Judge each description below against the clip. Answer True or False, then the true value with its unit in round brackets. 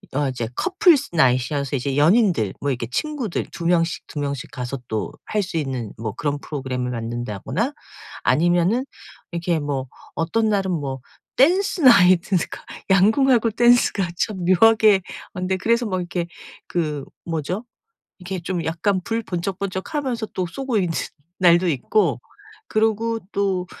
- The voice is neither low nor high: True (180 Hz)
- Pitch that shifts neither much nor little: False (7.1 semitones)